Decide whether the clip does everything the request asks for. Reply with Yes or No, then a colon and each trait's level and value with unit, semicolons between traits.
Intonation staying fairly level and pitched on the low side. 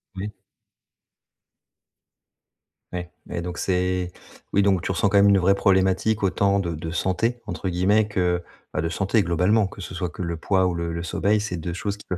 Yes: narrow, 2.3 semitones; very low, 95 Hz